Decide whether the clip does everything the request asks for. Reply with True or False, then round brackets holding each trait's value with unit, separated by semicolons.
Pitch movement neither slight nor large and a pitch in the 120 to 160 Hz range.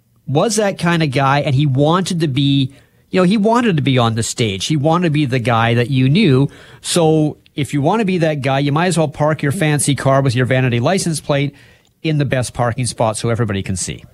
True (3.7 semitones; 140 Hz)